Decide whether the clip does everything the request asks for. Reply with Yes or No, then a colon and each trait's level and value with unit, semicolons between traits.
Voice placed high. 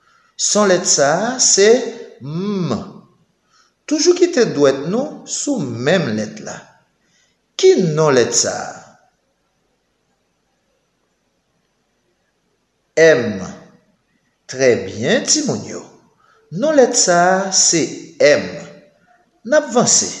Yes: high, 225 Hz